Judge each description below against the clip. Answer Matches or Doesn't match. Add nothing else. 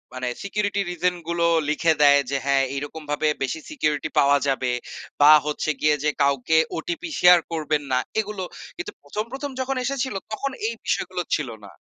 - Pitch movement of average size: Doesn't match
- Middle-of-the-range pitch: Matches